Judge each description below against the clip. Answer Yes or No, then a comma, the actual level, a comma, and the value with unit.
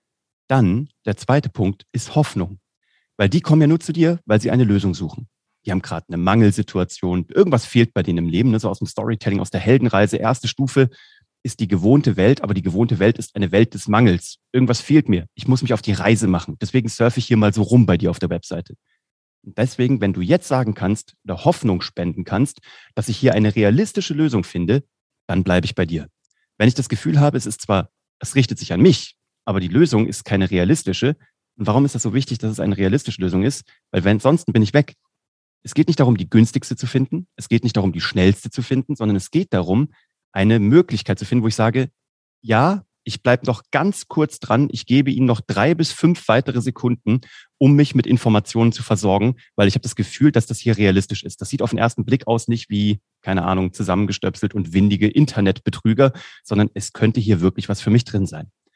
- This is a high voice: No, low, 115 Hz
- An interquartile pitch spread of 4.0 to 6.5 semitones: Yes, average, 4.6 semitones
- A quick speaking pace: Yes, fast, 225 wpm